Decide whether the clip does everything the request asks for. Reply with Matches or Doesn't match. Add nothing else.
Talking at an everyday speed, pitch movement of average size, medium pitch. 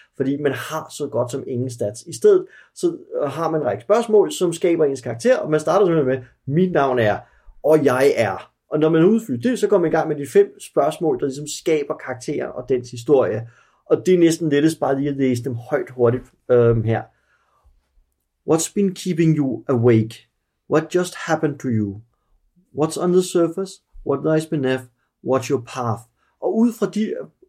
Doesn't match